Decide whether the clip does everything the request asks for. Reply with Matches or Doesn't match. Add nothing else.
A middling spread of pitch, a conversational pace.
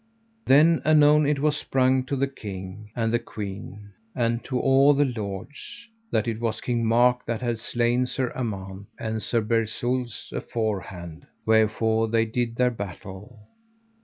Matches